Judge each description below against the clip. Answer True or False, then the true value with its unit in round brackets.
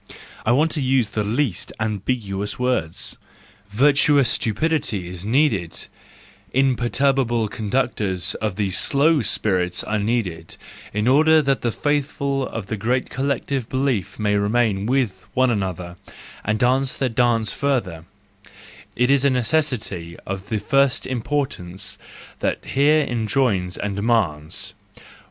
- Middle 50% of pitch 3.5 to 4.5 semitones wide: False (5.0 semitones)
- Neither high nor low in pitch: False (115 Hz)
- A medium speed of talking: False (130 wpm)